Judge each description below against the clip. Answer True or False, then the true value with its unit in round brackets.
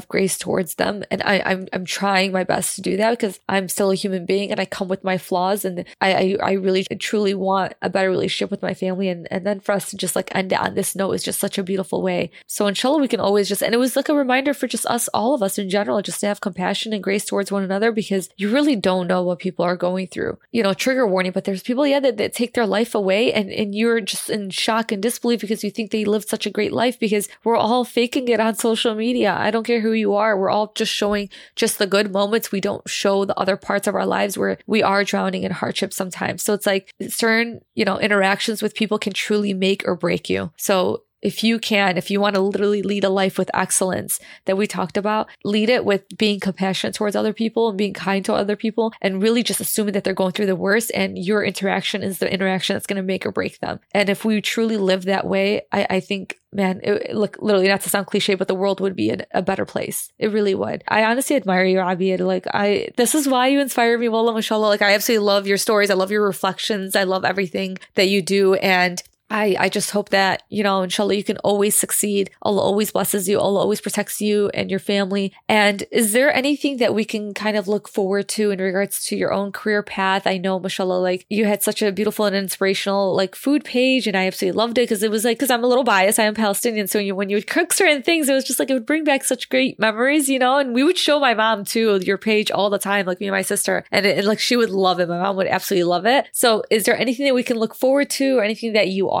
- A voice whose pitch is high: True (205 Hz)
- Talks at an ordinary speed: False (265 wpm)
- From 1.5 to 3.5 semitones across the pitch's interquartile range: True (2.6 semitones)